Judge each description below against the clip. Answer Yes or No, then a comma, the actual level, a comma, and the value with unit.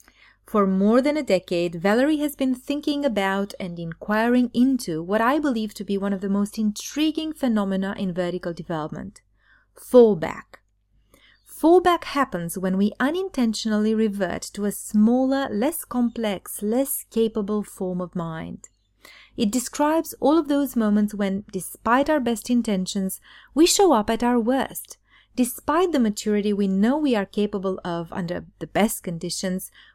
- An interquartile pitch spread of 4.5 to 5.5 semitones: Yes, average, 5.0 semitones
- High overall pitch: Yes, high, 215 Hz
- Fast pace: No, average, 150 wpm